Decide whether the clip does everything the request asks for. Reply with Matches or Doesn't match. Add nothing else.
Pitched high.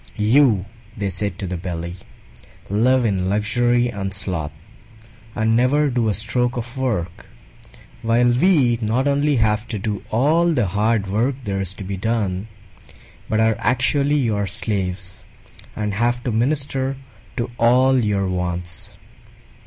Doesn't match